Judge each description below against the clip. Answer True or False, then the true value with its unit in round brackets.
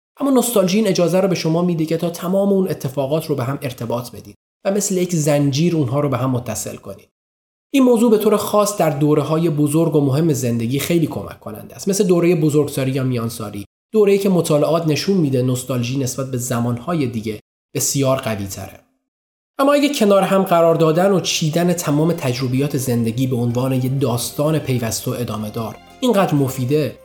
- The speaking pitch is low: False (150 Hz)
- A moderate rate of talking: False (180 wpm)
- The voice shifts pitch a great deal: True (5.9 semitones)